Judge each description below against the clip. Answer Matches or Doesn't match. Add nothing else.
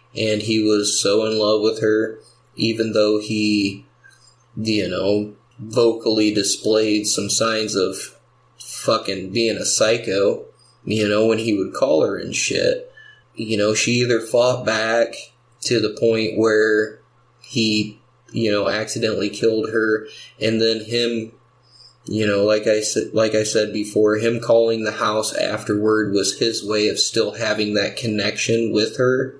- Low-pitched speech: Matches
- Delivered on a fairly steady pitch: Matches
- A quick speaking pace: Doesn't match